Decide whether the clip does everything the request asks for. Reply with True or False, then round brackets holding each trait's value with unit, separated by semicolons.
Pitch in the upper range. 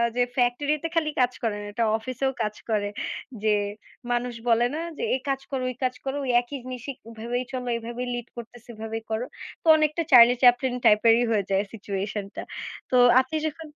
True (245 Hz)